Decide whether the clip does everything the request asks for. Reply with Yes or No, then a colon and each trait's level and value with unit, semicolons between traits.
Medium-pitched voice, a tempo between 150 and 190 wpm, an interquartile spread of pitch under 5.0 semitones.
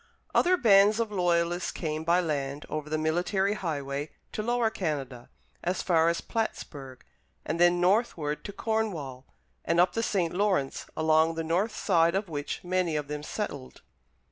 Yes: medium, 170 Hz; average, 160 wpm; average, 4.6 semitones